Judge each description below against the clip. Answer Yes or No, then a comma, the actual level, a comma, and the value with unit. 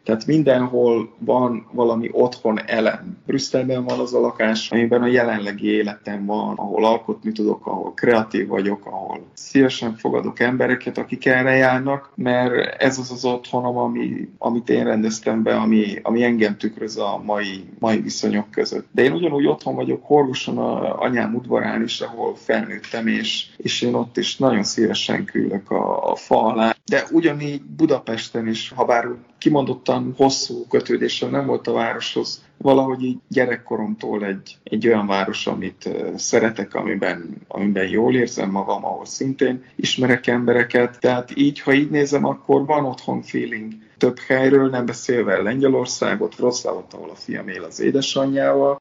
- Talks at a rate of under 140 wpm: No, average, 150 wpm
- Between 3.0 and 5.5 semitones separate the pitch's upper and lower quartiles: Yes, average, 3.5 semitones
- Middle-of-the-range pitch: No, low, 120 Hz